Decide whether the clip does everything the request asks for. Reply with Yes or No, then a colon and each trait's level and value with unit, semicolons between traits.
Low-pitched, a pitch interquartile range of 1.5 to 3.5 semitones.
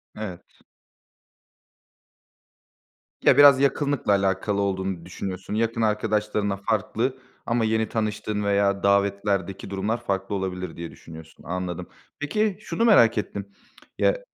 Yes: low, 100 Hz; average, 2.7 semitones